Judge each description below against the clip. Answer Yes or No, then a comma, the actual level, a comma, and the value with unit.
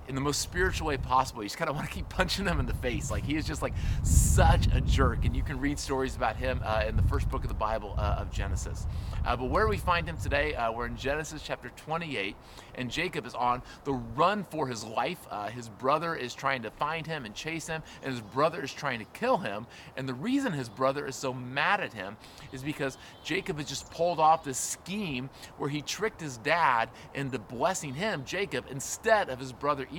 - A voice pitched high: No, low, 135 Hz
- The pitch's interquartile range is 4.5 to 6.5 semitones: Yes, average, 5.1 semitones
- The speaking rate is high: Yes, fast, 235 wpm